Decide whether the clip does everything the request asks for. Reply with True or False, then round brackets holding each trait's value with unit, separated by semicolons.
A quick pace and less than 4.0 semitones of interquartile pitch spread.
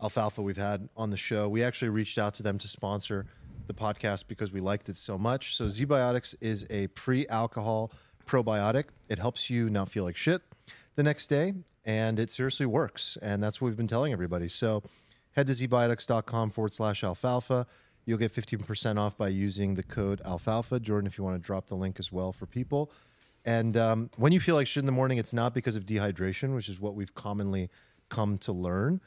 True (210 wpm; 3.5 semitones)